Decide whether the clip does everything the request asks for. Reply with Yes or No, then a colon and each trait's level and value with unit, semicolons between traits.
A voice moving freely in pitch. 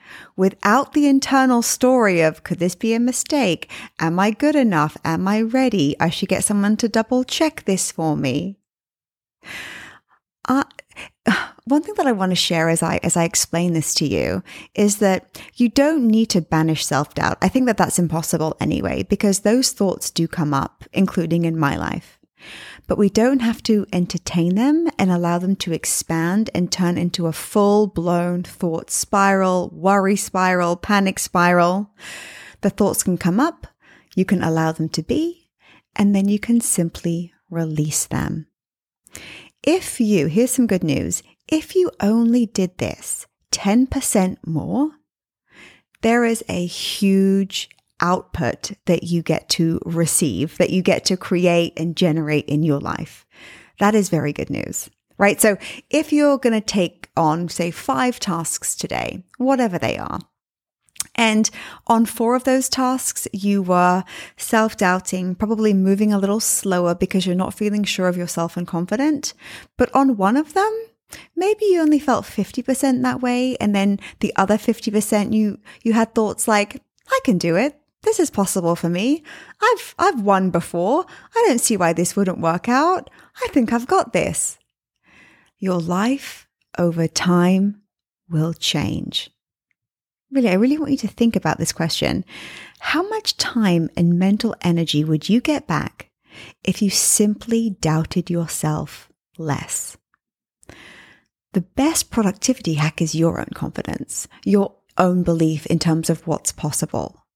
Yes: wide, 5.8 semitones